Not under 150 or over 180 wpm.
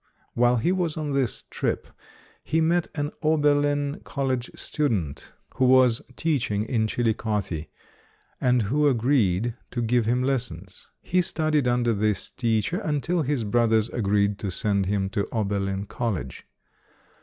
No: average, 140 wpm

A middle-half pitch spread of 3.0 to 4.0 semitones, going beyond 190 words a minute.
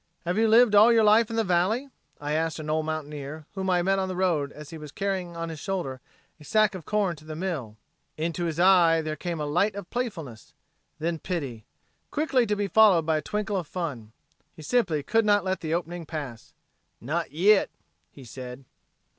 No: average, 4.7 semitones; fast, 205 wpm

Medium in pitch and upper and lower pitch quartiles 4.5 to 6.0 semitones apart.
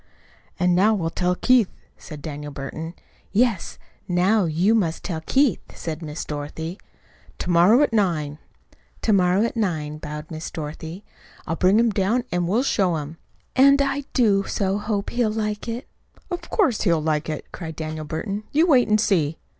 Yes: medium, 180 Hz; wide, 5.5 semitones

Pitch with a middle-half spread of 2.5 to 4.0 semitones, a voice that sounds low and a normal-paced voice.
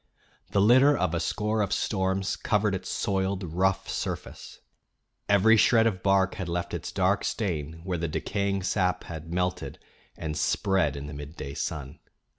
Yes: average, 3.1 semitones; very low, 95 Hz; average, 160 wpm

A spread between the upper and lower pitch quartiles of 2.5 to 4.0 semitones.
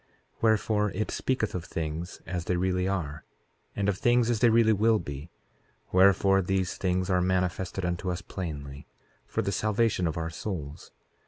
Yes: average, 3.3 semitones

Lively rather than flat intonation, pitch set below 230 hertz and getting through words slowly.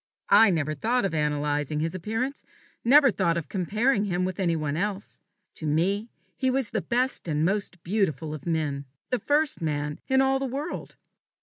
No: wide, 7.6 semitones; medium, 185 Hz; average, 180 wpm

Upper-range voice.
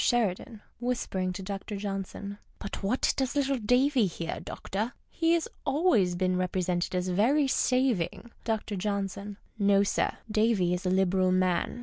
Yes: high, 200 Hz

